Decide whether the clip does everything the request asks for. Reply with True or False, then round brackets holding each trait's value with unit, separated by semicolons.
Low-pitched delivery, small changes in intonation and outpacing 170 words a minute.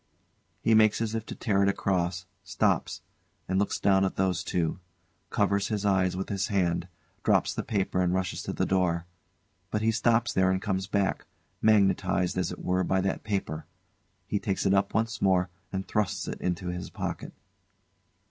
True (95 Hz; 1.9 semitones; 180 wpm)